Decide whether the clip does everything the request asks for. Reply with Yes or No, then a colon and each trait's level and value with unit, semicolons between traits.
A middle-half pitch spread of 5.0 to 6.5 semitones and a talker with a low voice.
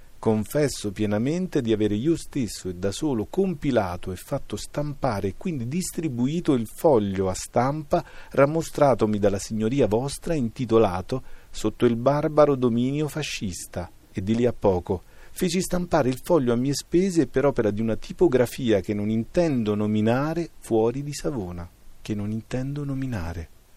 Yes: wide, 5.6 semitones; low, 120 Hz